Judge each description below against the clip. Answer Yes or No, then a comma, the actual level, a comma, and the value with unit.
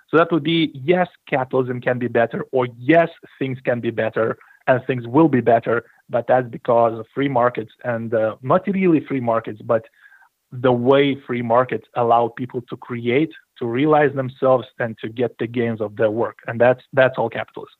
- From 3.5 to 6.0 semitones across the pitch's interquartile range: No, average, 2.7 semitones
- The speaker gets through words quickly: No, average, 190 wpm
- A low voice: Yes, low, 125 Hz